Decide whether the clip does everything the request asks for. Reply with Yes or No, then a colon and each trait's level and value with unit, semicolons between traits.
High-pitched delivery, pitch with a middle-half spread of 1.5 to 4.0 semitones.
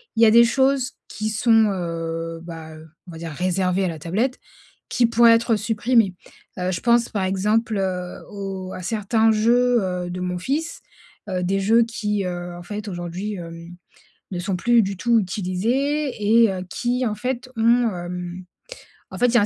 No: high, 200 Hz; average, 4.4 semitones